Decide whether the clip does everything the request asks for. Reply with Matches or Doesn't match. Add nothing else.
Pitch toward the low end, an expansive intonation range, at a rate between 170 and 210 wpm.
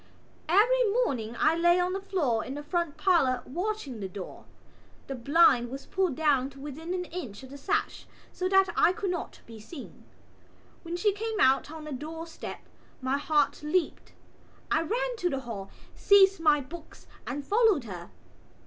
Doesn't match